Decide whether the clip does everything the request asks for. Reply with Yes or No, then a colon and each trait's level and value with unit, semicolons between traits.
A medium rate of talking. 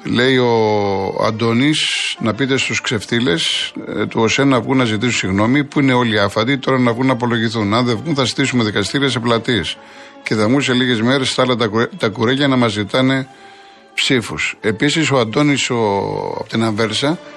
No: fast, 180 wpm